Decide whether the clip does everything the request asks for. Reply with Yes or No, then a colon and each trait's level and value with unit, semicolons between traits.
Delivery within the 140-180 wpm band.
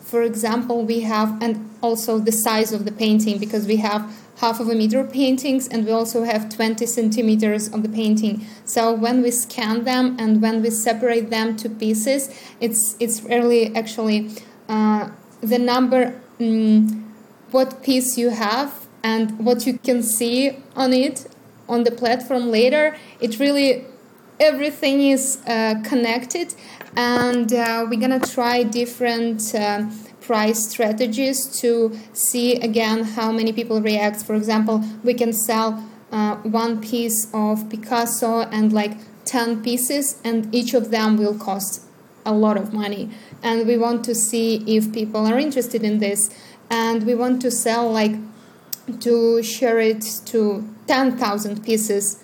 Yes: average, 155 wpm